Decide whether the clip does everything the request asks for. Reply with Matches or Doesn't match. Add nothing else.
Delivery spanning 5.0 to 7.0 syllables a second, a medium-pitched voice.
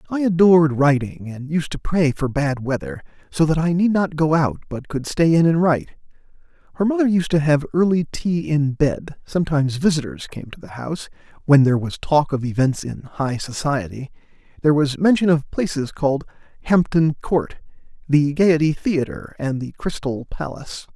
Matches